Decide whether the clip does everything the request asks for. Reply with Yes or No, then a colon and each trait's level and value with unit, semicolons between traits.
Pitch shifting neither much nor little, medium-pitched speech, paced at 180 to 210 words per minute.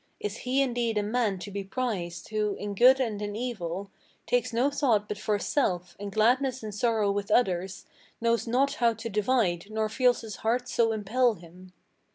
No: average, 3.4 semitones; high, 215 Hz; average, 190 wpm